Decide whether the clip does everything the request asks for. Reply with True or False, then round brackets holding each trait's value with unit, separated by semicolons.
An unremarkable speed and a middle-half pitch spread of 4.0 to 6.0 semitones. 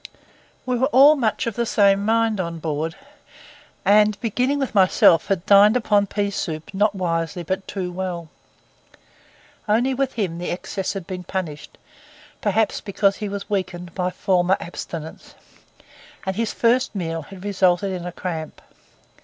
False (155 wpm; 3.2 semitones)